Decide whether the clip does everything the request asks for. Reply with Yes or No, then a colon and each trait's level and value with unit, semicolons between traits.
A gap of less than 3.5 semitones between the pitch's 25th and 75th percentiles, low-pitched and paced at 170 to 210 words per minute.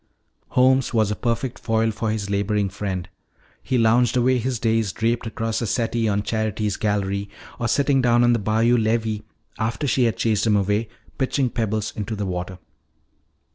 Yes: narrow, 2.4 semitones; low, 110 Hz; average, 175 wpm